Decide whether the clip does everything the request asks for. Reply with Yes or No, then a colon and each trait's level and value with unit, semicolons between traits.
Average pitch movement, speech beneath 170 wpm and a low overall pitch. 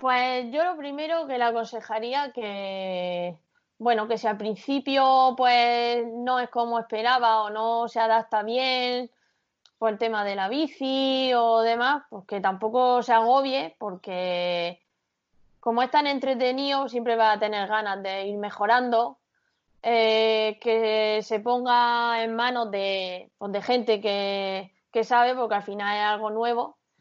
No: average, 3.0 semitones; average, 150 wpm; high, 230 Hz